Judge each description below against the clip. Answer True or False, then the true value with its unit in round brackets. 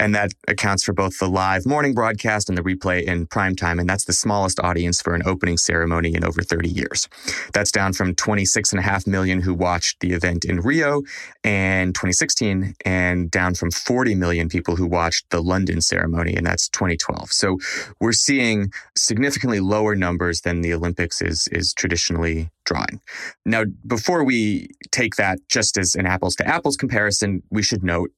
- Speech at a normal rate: True (190 wpm)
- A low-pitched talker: True (95 Hz)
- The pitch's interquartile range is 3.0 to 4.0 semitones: True (3.3 semitones)